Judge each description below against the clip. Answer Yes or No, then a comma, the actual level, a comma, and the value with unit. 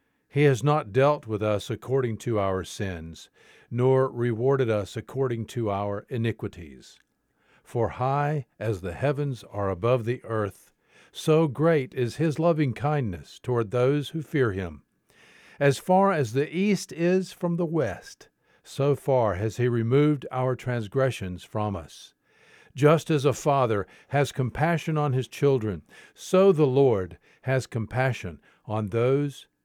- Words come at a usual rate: Yes, average, 145 wpm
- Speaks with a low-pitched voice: Yes, low, 130 Hz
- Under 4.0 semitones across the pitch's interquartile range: No, average, 5.1 semitones